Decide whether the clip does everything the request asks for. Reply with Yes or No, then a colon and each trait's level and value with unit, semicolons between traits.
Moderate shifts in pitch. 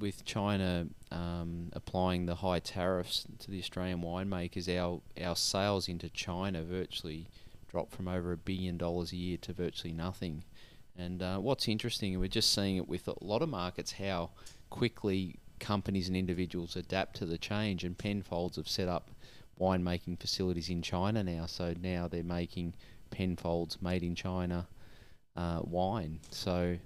No: narrow, 2.0 semitones